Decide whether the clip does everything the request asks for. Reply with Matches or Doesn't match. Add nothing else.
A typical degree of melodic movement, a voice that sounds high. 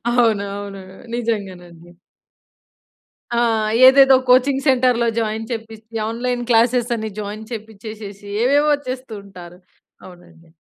Matches